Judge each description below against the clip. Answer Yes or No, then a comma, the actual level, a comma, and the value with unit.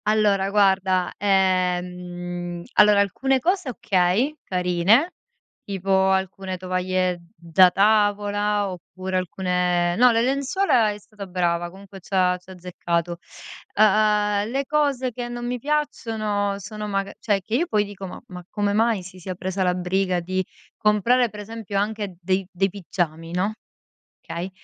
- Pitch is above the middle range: Yes, high, 195 Hz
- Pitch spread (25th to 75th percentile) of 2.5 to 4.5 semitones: Yes, average, 2.8 semitones